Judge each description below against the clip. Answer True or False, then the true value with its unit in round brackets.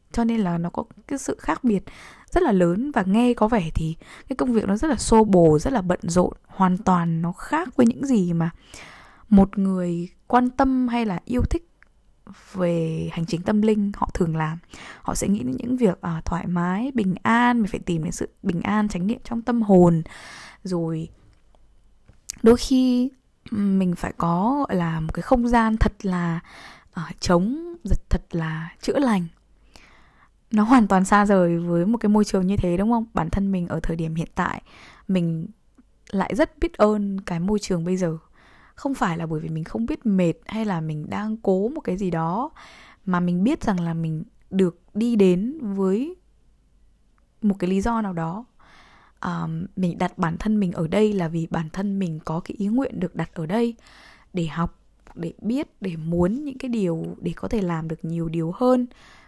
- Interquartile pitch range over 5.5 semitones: False (5.2 semitones)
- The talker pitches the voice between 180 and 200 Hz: True (190 Hz)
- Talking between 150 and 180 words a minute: False (200 wpm)